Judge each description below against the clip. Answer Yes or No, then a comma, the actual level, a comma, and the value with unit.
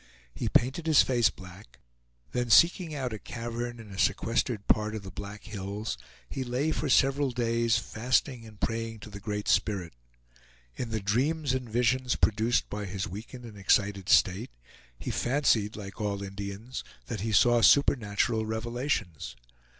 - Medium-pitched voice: No, low, 115 Hz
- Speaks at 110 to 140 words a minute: No, average, 160 wpm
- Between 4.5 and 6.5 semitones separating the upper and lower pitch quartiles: No, average, 3.3 semitones